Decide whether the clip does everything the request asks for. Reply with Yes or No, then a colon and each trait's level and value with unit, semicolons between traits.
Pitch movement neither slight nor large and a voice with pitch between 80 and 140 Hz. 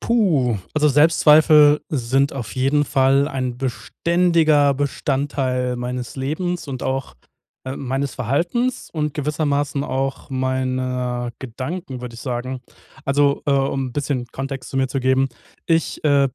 No: narrow, 2.3 semitones; low, 135 Hz